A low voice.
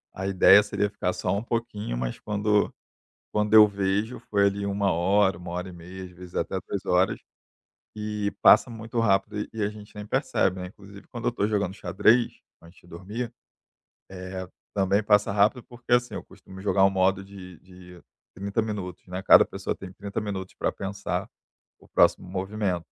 Yes: low, 100 Hz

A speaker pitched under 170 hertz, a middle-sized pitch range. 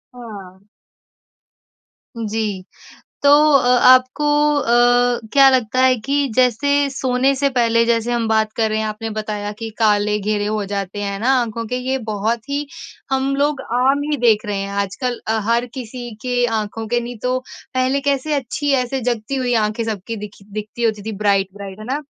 No: high, 235 Hz; average, 3.3 semitones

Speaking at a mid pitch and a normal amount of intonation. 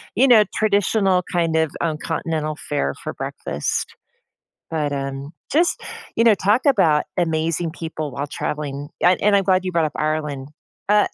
Yes: medium, 160 Hz; average, 4.4 semitones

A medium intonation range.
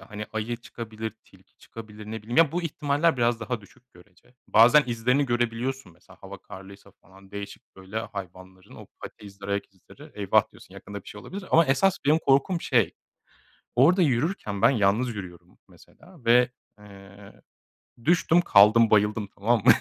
Yes: average, 5.0 semitones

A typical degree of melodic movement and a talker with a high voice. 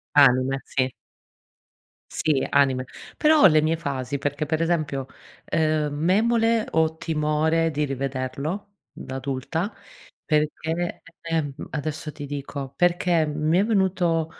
No: average, 3.1 semitones; medium, 155 Hz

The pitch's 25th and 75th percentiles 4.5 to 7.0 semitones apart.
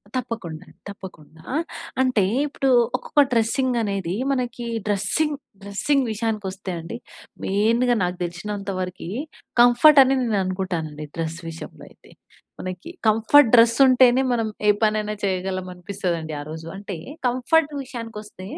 Yes: average, 4.9 semitones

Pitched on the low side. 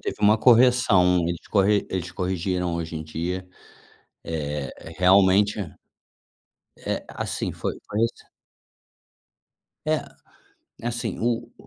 Yes: very low, 95 Hz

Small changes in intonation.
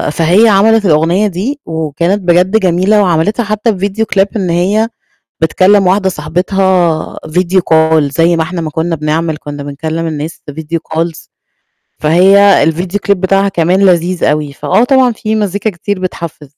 No: average, 3.7 semitones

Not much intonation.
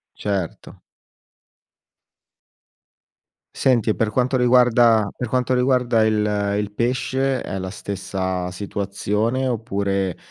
No: average, 3.8 semitones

